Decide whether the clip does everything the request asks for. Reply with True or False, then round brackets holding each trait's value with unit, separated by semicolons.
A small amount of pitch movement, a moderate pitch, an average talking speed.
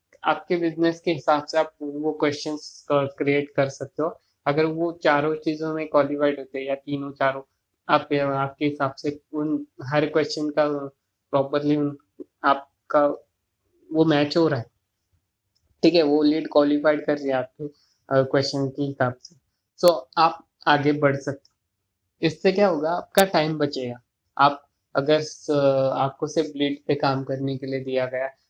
True (2.2 semitones; 145 Hz; 160 wpm)